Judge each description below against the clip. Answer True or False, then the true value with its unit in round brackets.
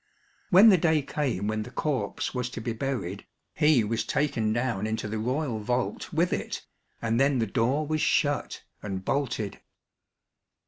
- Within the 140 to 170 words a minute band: True (165 wpm)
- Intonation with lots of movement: False (4.9 semitones)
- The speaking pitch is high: False (125 Hz)